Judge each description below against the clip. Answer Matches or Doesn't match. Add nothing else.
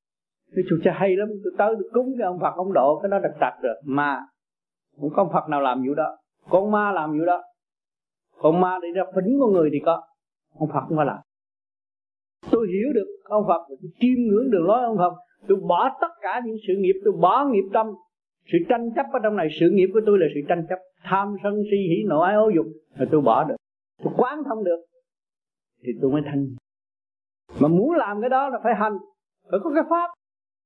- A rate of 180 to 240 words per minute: Matches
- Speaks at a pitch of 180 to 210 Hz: Matches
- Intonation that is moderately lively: Doesn't match